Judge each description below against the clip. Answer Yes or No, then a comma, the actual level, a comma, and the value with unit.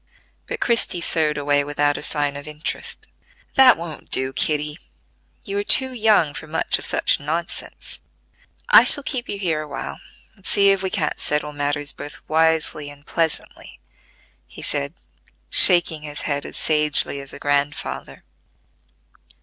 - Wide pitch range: No, average, 3.2 semitones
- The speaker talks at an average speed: Yes, average, 155 wpm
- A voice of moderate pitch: Yes, medium, 150 Hz